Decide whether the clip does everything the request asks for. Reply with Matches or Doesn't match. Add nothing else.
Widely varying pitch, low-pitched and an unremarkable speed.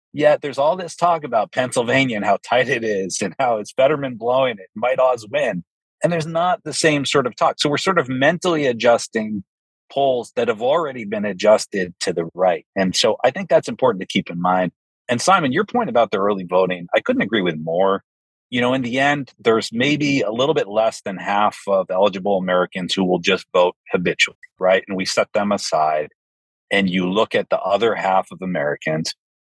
Doesn't match